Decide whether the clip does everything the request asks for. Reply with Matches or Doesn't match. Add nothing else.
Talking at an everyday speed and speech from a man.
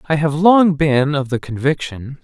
Matches